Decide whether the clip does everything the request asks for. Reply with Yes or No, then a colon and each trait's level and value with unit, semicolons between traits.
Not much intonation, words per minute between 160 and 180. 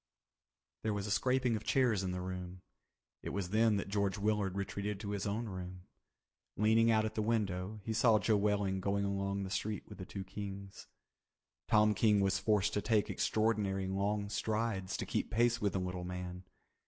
No: narrow, 2.1 semitones; average, 190 wpm